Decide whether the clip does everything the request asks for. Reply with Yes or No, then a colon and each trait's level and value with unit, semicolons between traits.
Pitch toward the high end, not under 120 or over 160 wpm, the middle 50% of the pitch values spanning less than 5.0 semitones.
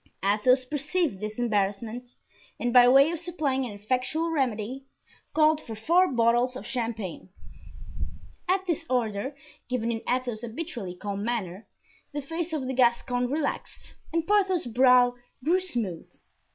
No: very high, 250 Hz; average, 140 wpm; wide, 5.4 semitones